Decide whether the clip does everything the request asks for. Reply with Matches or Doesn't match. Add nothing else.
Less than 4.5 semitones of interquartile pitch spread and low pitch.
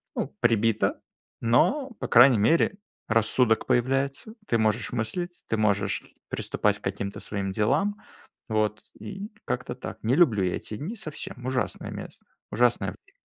Doesn't match